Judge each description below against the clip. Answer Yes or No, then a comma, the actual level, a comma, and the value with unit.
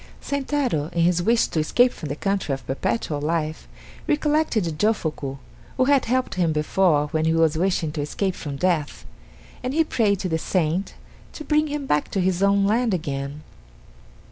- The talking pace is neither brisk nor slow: Yes, average, 175 wpm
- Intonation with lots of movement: Yes, wide, 7.2 semitones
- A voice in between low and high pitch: Yes, medium, 180 Hz